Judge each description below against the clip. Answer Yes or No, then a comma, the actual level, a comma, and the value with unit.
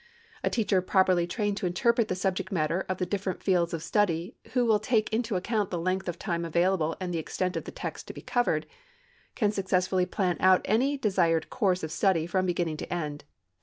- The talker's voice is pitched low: No, medium, 185 Hz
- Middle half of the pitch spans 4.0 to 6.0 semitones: No, average, 3.1 semitones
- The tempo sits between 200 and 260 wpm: Yes, fast, 205 wpm